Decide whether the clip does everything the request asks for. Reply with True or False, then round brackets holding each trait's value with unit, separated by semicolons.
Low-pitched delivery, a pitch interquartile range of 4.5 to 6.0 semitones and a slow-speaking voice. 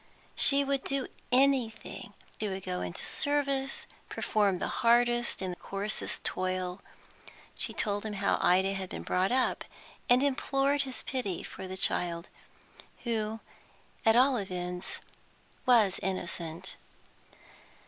False (210 Hz; 5.6 semitones; 120 wpm)